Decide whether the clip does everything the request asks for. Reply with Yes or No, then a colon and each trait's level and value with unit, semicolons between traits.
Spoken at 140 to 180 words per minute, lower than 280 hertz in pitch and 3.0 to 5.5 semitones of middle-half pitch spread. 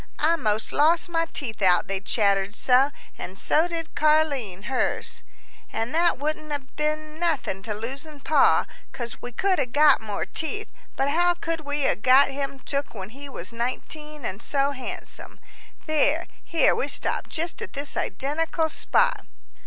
No: average, 165 wpm; very high, 285 Hz; average, 5.1 semitones